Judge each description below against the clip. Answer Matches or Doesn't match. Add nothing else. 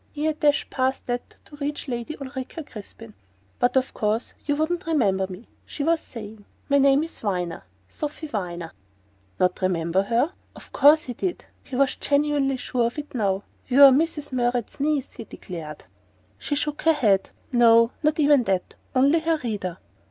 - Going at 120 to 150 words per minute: Doesn't match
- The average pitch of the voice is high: Matches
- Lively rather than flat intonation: Matches